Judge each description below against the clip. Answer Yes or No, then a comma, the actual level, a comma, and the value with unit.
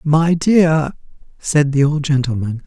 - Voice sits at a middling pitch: Yes, medium, 150 Hz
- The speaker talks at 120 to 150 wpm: Yes, slow, 135 wpm